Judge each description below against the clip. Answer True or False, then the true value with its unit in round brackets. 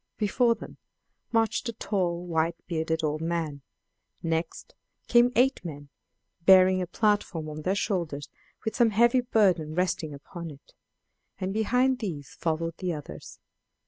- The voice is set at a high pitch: False (175 Hz)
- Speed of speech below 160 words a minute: True (140 wpm)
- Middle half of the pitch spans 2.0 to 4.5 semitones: False (5.3 semitones)